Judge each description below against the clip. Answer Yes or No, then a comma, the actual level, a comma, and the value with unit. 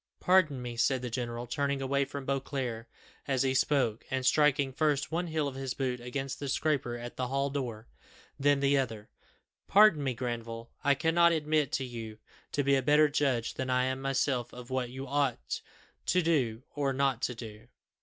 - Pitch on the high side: No, low, 135 Hz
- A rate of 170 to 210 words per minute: Yes, average, 185 wpm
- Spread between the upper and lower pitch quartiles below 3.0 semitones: Yes, narrow, 2.6 semitones